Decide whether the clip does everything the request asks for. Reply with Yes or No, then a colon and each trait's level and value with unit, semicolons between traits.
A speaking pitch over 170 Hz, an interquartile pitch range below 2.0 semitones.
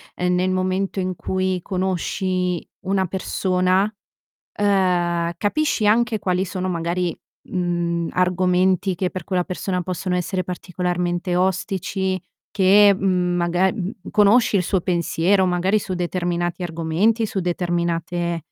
Yes: medium, 185 Hz; narrow, 1.4 semitones